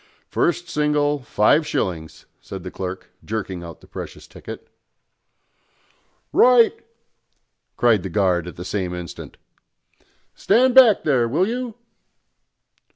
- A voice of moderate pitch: No, low, 115 Hz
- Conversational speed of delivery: No, slow, 115 wpm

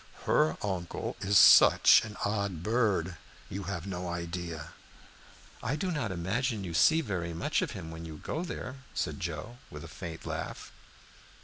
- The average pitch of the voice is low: Yes, very low, 90 Hz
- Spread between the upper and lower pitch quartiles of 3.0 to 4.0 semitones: No, average, 4.6 semitones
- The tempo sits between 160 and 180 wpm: Yes, average, 170 wpm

